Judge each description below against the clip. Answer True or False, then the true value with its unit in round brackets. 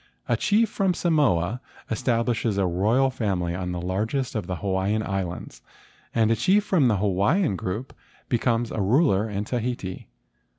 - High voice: False (110 Hz)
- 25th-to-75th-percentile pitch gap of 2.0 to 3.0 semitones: False (5.2 semitones)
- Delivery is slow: False (155 wpm)